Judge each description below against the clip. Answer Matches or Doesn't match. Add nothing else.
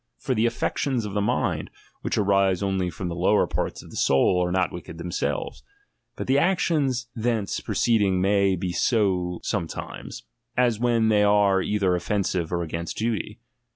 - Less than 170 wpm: Doesn't match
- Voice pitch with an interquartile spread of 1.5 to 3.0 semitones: Doesn't match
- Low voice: Matches